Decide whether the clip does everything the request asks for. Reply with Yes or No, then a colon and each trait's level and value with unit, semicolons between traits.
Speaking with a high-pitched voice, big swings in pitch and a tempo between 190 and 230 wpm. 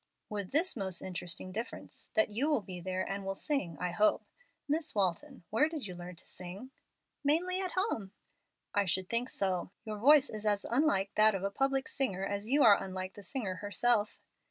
Yes: high, 205 Hz; wide, 6.3 semitones; average, 195 wpm